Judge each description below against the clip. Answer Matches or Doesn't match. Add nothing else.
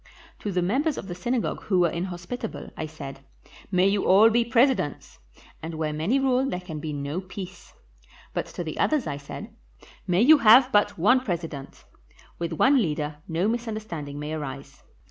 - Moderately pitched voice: Matches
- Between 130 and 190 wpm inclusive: Matches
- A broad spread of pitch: Matches